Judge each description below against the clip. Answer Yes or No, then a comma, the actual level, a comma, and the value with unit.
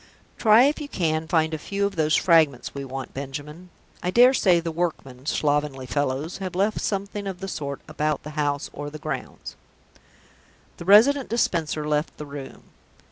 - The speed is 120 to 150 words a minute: No, average, 180 wpm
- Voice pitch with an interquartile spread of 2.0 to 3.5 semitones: No, average, 4.9 semitones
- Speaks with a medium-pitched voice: Yes, medium, 155 Hz